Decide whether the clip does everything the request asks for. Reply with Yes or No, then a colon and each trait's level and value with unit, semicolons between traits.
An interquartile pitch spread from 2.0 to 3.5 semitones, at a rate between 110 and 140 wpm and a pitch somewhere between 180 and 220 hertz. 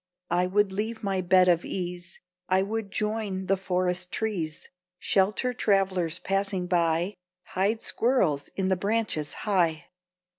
Yes: narrow, 2.6 semitones; slow, 135 wpm; high, 190 Hz